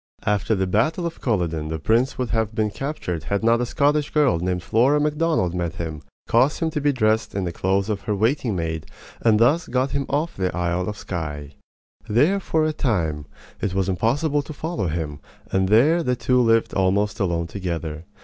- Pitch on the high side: No, low, 105 Hz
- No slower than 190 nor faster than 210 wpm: Yes, average, 200 wpm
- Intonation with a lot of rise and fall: Yes, wide, 7.6 semitones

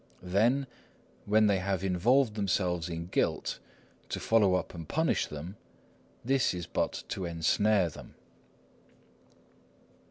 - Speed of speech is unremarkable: No, slow, 115 wpm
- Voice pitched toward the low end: Yes, very low, 95 Hz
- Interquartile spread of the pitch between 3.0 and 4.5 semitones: Yes, average, 3.8 semitones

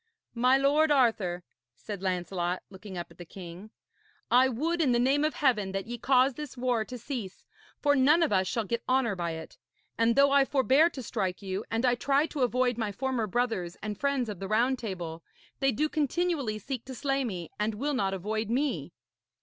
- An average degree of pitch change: No, wide, 5.7 semitones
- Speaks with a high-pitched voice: Yes, high, 240 Hz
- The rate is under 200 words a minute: No, fast, 205 wpm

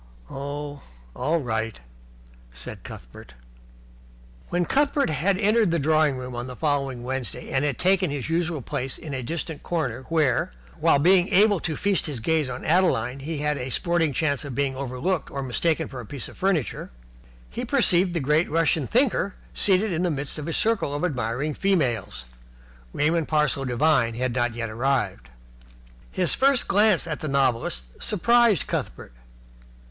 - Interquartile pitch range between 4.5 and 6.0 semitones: Yes, average, 5.3 semitones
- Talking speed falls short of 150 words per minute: No, average, 165 wpm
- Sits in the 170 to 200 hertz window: No, medium, 150 Hz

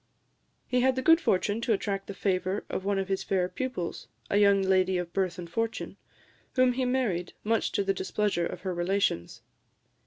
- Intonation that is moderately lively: Yes, average, 3.6 semitones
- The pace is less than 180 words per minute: No, average, 190 wpm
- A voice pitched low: No, high, 195 Hz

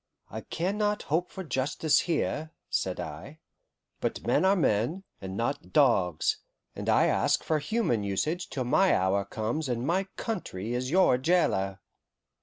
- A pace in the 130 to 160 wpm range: Yes, average, 155 wpm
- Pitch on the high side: No, medium, 140 Hz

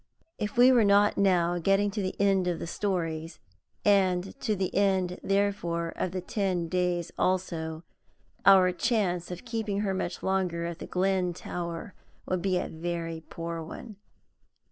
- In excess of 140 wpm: Yes, average, 160 wpm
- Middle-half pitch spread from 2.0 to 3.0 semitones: Yes, narrow, 2.6 semitones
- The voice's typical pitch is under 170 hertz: No, medium, 185 Hz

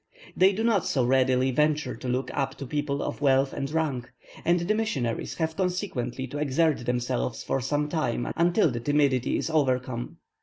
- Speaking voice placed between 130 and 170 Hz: Yes, medium, 140 Hz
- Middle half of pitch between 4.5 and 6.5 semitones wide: No, average, 4.1 semitones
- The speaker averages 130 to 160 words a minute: No, average, 180 wpm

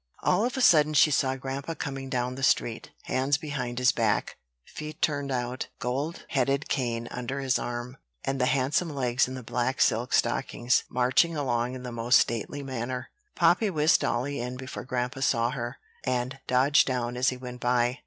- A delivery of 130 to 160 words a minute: No, average, 185 wpm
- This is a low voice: Yes, low, 130 Hz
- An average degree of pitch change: No, narrow, 2.2 semitones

